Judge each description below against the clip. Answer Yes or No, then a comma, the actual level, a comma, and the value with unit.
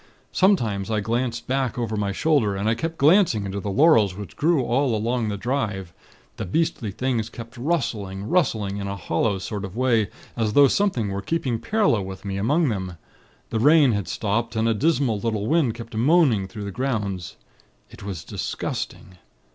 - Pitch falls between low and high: No, low, 115 Hz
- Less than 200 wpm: Yes, average, 180 wpm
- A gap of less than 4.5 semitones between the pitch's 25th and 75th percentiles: No, average, 5.0 semitones